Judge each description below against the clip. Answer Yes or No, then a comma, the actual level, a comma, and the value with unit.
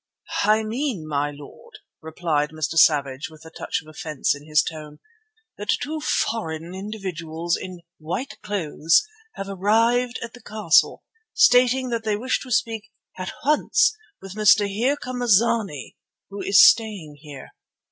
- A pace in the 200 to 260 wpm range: No, average, 155 wpm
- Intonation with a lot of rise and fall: Yes, wide, 6.6 semitones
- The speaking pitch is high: Yes, high, 195 Hz